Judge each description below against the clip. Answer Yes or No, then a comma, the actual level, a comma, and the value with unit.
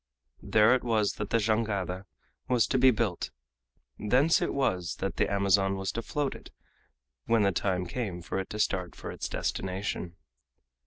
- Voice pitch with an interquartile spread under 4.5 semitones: Yes, average, 3.5 semitones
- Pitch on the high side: No, low, 105 Hz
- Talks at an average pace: Yes, average, 170 wpm